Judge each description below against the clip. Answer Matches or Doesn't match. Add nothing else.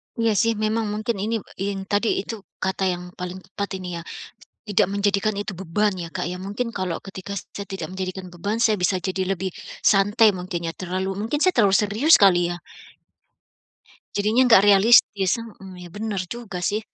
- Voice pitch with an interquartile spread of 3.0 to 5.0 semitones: Doesn't match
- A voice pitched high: Matches